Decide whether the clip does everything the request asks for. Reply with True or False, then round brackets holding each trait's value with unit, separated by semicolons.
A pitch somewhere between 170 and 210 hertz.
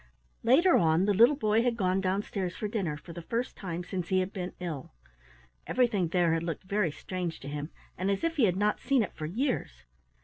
True (185 Hz)